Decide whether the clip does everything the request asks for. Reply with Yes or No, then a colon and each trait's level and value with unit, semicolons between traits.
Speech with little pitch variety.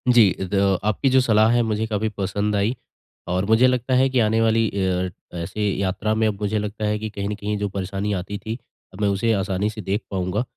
Yes: narrow, 2.0 semitones